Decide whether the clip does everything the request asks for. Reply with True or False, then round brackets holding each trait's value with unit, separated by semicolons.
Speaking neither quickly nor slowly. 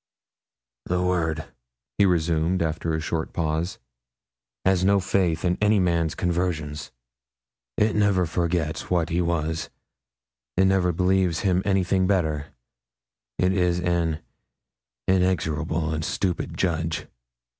False (115 wpm)